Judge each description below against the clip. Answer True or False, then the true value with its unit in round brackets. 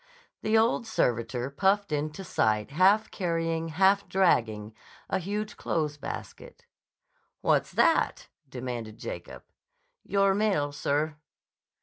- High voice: False (165 Hz)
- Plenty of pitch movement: True (7.0 semitones)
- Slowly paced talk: True (105 wpm)